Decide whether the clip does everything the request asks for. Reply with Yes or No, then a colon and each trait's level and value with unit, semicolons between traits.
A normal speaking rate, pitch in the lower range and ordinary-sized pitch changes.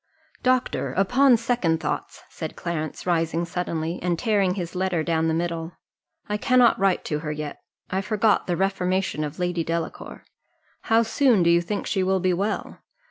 No: average, 170 wpm; medium, 180 Hz; average, 3.7 semitones